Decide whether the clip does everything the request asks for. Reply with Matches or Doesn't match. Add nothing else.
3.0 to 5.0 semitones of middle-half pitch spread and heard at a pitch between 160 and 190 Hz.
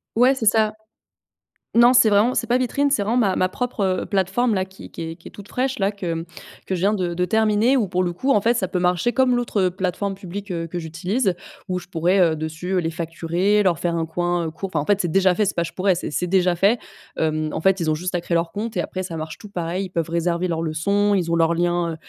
Matches